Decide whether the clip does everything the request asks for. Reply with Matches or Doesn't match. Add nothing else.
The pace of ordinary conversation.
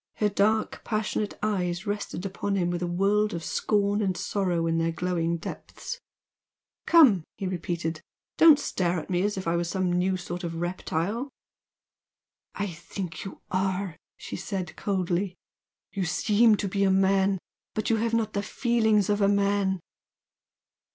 Matches